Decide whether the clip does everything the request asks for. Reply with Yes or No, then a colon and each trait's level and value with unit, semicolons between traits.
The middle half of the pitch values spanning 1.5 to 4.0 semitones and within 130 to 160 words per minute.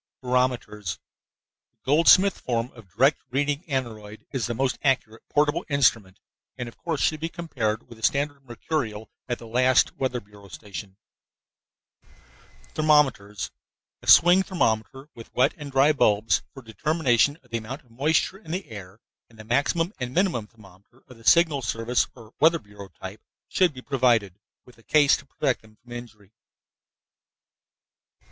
No: average, 4.8 semitones; average, 155 wpm